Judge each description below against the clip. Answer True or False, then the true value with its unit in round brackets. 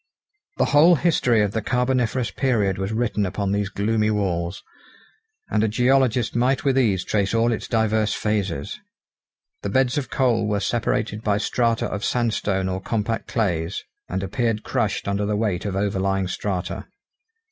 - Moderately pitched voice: False (105 Hz)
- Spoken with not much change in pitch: False (3.2 semitones)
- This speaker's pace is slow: False (160 wpm)